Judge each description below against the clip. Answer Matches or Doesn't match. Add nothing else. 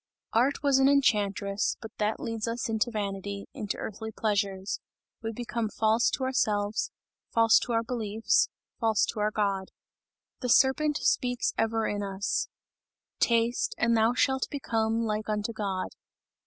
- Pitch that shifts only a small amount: Matches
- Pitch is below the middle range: Doesn't match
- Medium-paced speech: Matches